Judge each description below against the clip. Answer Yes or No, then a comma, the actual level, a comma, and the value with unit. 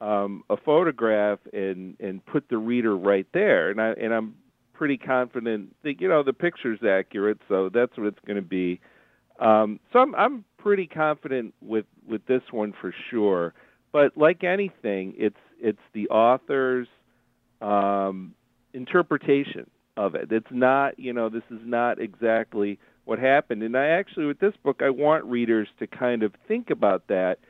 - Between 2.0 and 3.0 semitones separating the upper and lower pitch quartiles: No, average, 5.1 semitones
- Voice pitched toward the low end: Yes, low, 120 Hz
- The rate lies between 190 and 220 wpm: No, average, 170 wpm